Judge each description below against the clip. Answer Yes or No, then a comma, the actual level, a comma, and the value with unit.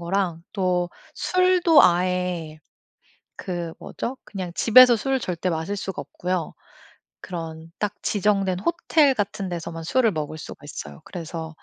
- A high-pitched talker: No, medium, 180 Hz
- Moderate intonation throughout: Yes, average, 4.0 semitones